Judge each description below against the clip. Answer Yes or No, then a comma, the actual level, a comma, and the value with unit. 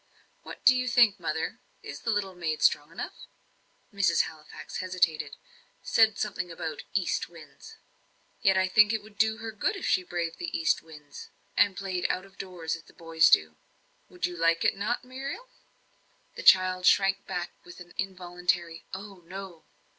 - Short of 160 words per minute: No, average, 170 wpm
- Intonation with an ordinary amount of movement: Yes, average, 3.7 semitones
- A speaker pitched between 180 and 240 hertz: Yes, medium, 185 Hz